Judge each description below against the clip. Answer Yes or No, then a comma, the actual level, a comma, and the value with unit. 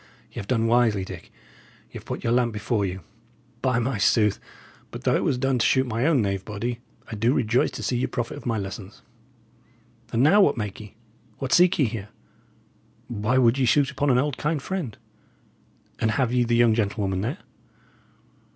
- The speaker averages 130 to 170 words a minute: No, average, 195 wpm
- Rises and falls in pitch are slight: No, average, 3.6 semitones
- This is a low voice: Yes, low, 120 Hz